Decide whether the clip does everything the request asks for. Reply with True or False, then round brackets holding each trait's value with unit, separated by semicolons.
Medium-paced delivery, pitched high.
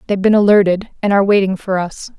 False (220 wpm; 195 Hz)